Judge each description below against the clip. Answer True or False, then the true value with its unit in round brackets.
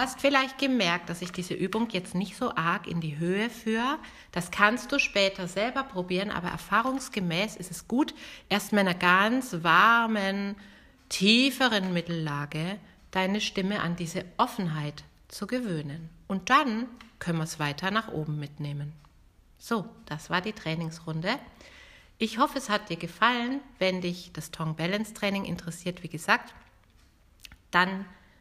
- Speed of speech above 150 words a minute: False (145 wpm)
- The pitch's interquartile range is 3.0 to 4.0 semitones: False (4.9 semitones)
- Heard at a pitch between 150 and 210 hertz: True (190 Hz)